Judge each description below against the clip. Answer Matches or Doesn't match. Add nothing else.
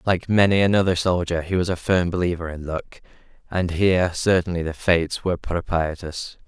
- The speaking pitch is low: Matches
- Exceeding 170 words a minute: Doesn't match